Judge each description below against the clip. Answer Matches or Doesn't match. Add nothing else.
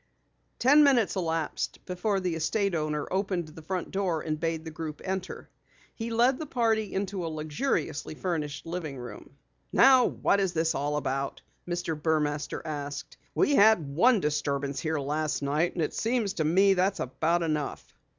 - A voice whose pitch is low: Doesn't match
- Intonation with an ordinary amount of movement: Matches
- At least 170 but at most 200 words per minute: Doesn't match